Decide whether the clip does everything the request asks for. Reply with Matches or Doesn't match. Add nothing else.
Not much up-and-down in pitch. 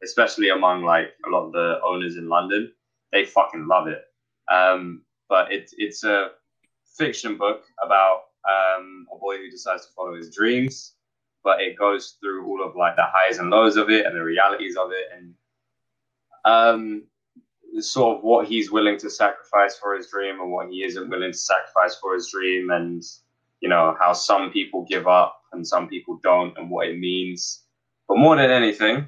Doesn't match